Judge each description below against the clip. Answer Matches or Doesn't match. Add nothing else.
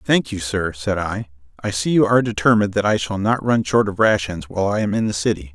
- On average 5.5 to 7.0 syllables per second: Matches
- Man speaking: Matches